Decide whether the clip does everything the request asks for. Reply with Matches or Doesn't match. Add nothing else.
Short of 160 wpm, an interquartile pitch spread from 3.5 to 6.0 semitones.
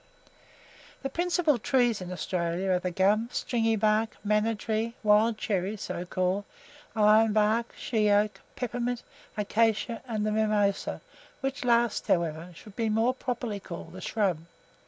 Doesn't match